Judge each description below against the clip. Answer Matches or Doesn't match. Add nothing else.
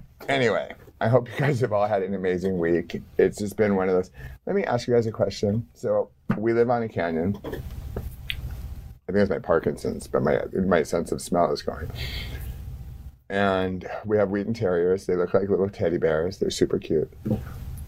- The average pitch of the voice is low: Matches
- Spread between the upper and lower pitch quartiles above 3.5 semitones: Matches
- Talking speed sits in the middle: Matches